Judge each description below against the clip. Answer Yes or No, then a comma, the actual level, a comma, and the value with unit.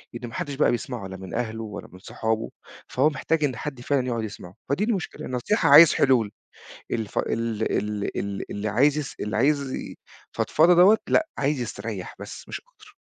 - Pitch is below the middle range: Yes, low, 125 Hz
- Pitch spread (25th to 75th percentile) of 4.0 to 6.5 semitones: Yes, average, 5.2 semitones